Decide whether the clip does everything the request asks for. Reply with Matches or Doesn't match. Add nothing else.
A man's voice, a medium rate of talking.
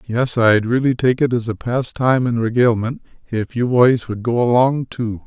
Matches